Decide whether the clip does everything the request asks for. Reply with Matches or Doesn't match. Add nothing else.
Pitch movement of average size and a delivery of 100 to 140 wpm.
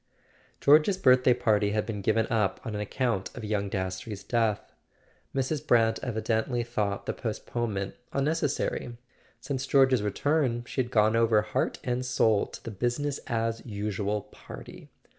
Doesn't match